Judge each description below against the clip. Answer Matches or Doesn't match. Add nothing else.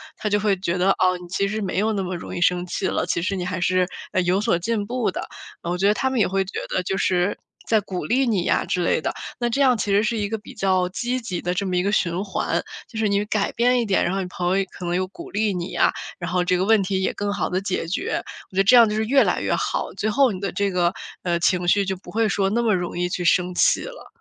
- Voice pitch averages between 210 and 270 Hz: Doesn't match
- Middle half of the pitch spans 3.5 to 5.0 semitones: Doesn't match